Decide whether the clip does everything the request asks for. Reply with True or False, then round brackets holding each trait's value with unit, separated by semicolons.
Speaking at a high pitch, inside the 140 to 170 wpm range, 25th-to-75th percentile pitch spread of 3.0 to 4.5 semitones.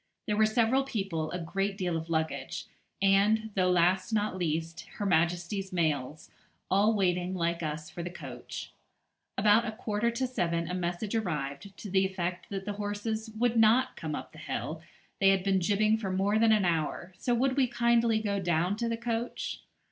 False (195 Hz; 185 wpm; 4.1 semitones)